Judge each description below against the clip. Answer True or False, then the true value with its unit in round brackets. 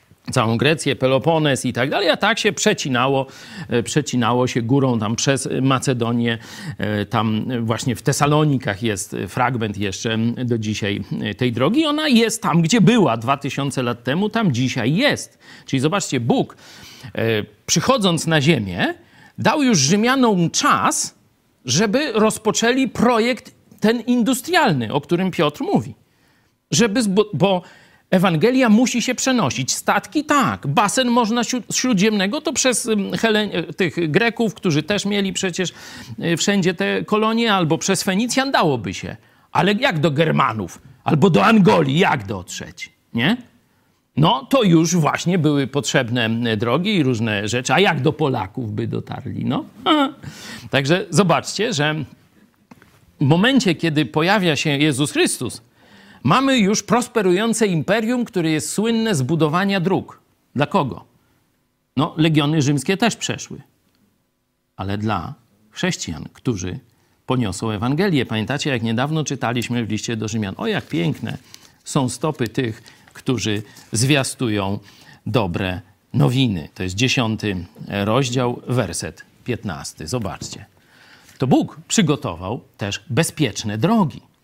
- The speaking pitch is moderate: True (150 Hz)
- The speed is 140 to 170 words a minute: False (125 wpm)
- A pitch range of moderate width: False (8.9 semitones)